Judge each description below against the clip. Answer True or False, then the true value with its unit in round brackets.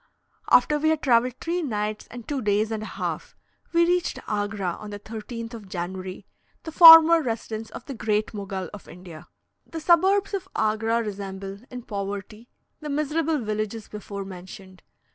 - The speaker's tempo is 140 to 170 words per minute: True (160 wpm)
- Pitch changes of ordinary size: False (6.6 semitones)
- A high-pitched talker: True (220 Hz)